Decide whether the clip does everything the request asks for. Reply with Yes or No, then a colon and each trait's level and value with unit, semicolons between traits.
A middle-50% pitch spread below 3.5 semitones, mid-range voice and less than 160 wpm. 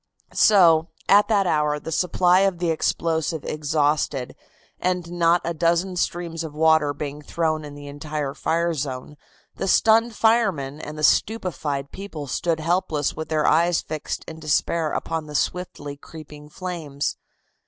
Yes: average, 2.9 semitones; medium, 160 Hz; average, 150 wpm